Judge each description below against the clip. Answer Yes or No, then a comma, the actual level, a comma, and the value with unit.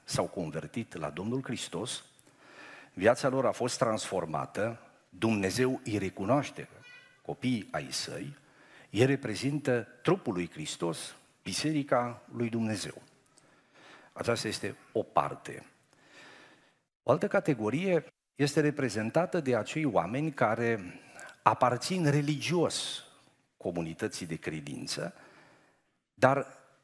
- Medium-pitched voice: No, low, 120 Hz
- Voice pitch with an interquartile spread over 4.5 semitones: Yes, average, 4.9 semitones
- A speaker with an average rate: No, slow, 95 wpm